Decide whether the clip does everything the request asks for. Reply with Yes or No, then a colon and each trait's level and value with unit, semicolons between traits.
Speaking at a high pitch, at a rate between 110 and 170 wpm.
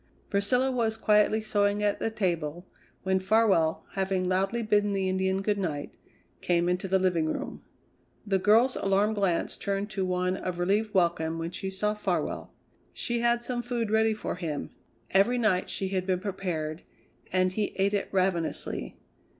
Yes: high, 195 Hz; average, 165 wpm